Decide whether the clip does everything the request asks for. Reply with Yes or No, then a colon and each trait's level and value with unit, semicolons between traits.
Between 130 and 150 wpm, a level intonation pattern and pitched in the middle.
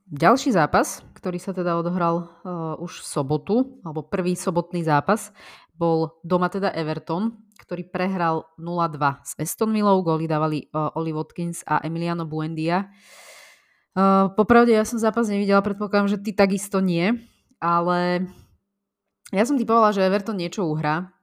No: average, 145 wpm; average, 3.7 semitones; medium, 180 Hz